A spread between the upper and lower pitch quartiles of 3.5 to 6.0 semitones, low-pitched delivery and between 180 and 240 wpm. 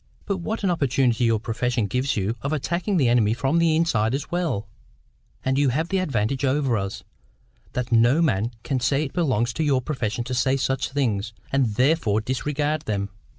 Yes: average, 4.6 semitones; low, 130 Hz; average, 190 wpm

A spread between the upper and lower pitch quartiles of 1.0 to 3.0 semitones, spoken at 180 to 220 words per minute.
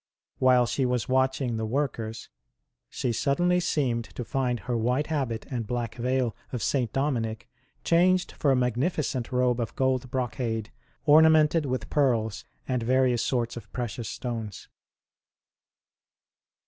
No: narrow, 2.5 semitones; slow, 135 wpm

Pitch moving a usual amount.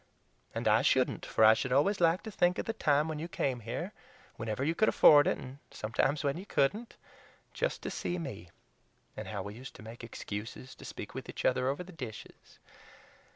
No: wide, 6.4 semitones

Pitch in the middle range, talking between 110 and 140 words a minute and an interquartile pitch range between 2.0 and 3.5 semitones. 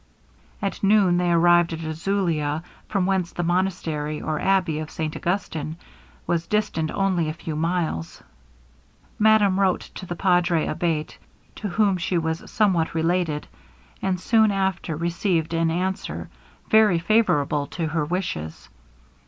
Yes: medium, 175 Hz; slow, 135 wpm; average, 3.1 semitones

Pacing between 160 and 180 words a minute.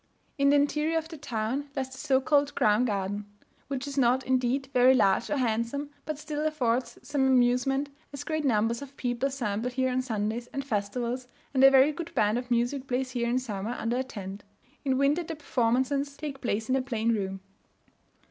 No: average, 195 wpm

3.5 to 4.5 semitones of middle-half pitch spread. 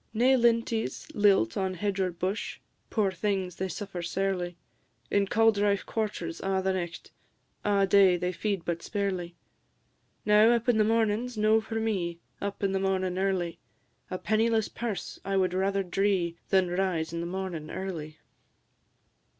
No: average, 2.8 semitones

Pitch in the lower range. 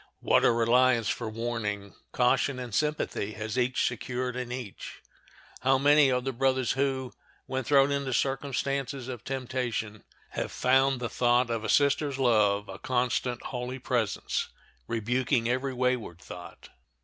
Yes: low, 125 Hz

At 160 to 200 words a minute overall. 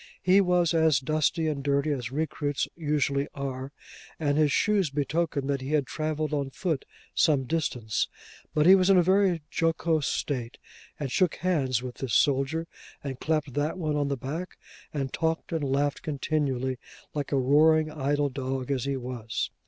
Yes: average, 170 wpm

